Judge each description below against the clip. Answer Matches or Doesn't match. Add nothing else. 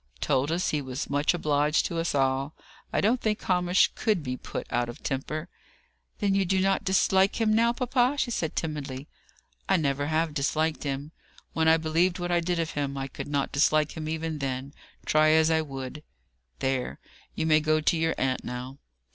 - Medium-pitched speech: Matches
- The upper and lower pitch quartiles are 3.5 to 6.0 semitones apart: Matches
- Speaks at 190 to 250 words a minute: Matches